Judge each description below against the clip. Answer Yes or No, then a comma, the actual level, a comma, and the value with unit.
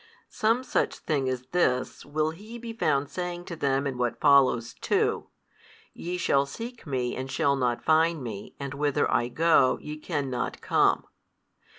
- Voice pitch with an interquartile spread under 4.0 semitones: No, average, 4.6 semitones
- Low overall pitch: No, medium, 145 Hz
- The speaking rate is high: No, average, 165 wpm